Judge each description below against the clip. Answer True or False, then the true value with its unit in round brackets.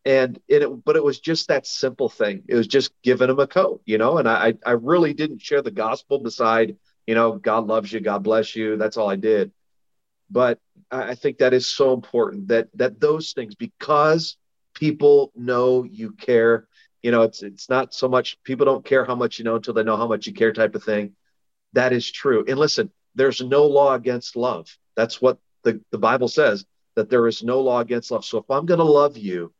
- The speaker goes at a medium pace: False (220 wpm)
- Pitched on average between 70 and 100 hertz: False (125 Hz)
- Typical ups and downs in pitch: True (4.7 semitones)